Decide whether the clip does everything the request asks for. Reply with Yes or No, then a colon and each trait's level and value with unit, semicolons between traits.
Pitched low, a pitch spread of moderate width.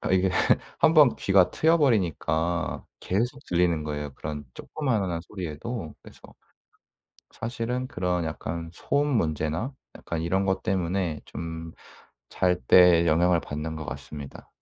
Yes: very low, 90 Hz; average, 4.8 semitones